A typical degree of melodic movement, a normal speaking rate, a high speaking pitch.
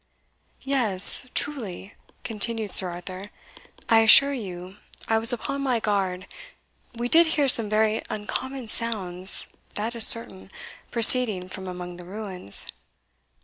No: average, 4.1 semitones; slow, 125 wpm; high, 215 Hz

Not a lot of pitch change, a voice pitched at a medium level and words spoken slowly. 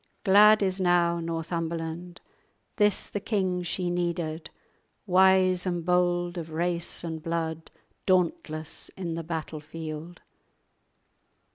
Yes: narrow, 2.0 semitones; medium, 175 Hz; slow, 110 wpm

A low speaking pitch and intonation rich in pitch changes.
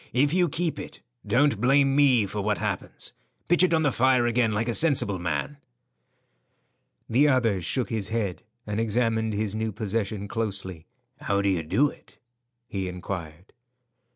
No: low, 110 Hz; average, 4.9 semitones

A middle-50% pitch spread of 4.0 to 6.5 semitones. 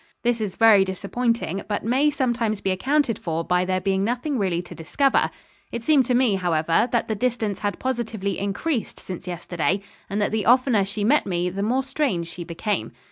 Yes: average, 4.7 semitones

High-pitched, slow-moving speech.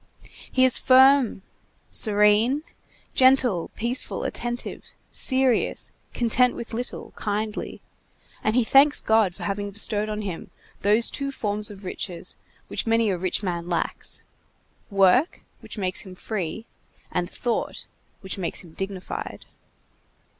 Yes: high, 215 Hz; slow, 125 wpm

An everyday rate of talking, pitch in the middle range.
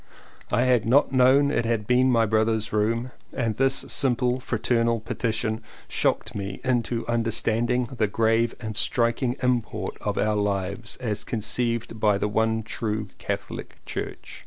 No: average, 150 wpm; low, 115 Hz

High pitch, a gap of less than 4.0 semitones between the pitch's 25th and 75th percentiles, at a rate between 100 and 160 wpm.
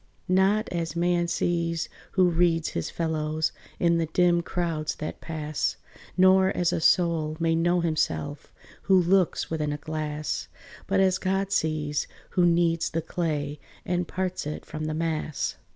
No: medium, 165 Hz; narrow, 2.4 semitones; average, 150 wpm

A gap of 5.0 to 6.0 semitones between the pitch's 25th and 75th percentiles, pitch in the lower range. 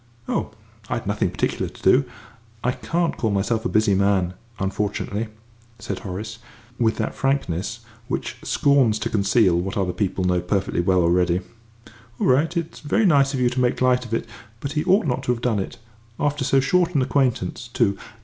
Yes: wide, 5.5 semitones; low, 115 Hz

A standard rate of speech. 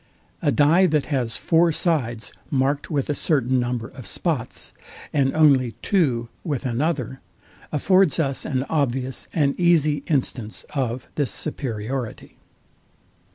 No: slow, 125 wpm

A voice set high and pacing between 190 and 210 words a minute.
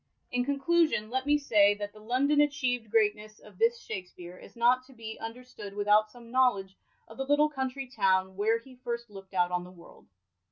Yes: high, 230 Hz; average, 195 wpm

